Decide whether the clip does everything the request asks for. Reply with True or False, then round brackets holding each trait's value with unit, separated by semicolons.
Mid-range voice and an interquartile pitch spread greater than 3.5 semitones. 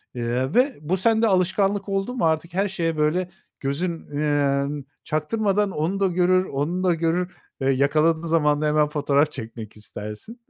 True (165 Hz; 4.4 semitones)